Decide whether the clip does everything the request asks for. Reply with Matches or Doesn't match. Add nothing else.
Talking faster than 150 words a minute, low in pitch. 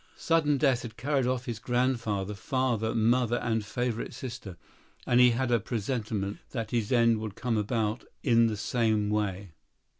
Matches